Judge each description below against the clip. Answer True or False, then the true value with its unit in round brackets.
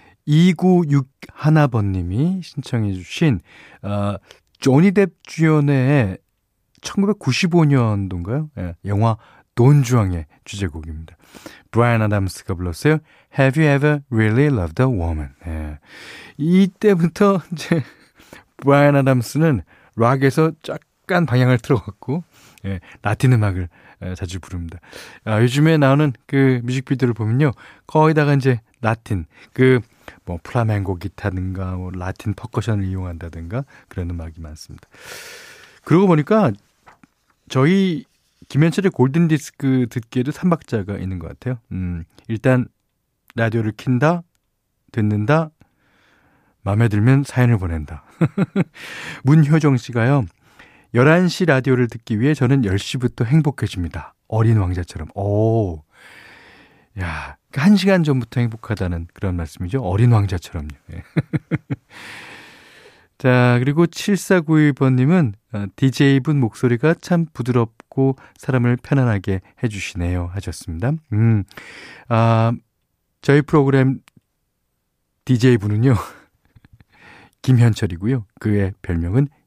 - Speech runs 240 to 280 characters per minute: True (255 characters per minute)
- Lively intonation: True (6.5 semitones)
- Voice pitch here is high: False (120 Hz)